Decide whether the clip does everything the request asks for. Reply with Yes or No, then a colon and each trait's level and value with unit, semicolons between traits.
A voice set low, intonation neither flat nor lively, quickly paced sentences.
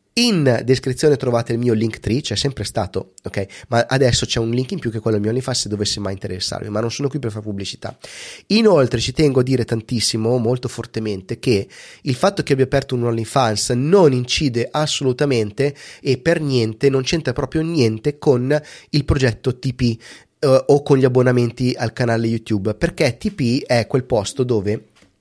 Yes: low, 125 Hz; average, 3.6 semitones; fast, 190 wpm